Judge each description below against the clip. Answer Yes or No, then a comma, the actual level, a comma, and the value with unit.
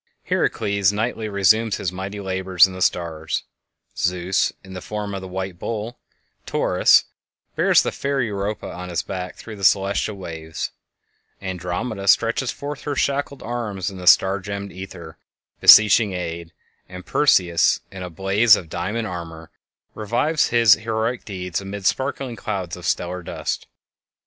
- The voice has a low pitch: Yes, very low, 95 Hz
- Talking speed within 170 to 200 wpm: No, average, 150 wpm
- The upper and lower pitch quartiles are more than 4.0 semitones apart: No, average, 3.3 semitones